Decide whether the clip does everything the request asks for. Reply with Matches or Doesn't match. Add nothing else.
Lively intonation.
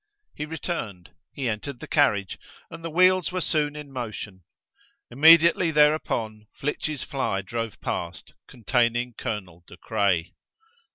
Matches